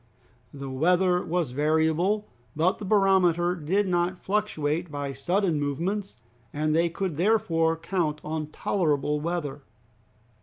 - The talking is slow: Yes, slow, 120 wpm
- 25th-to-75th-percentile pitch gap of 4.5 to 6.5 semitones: No, average, 3.6 semitones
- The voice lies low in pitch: No, medium, 170 Hz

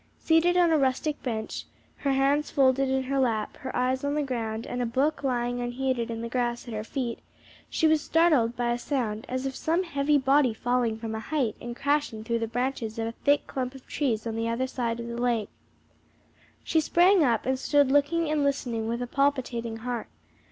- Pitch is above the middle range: Yes, very high, 255 Hz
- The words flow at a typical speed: No, fast, 210 wpm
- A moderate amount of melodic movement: Yes, average, 3.4 semitones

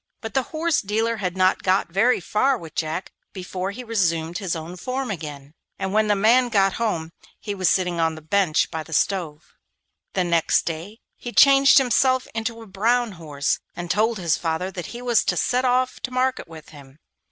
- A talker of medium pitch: No, high, 195 Hz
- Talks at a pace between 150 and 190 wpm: No, average, 200 wpm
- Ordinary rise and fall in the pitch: No, wide, 6.0 semitones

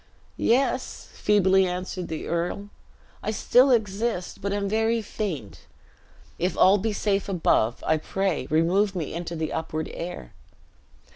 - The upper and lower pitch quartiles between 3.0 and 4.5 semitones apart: Yes, average, 3.7 semitones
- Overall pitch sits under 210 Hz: Yes, high, 190 Hz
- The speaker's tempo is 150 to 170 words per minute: No, slow, 135 wpm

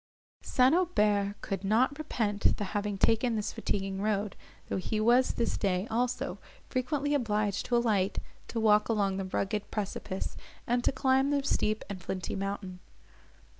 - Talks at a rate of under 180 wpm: Yes, average, 155 wpm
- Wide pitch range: No, average, 3.8 semitones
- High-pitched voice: Yes, high, 210 Hz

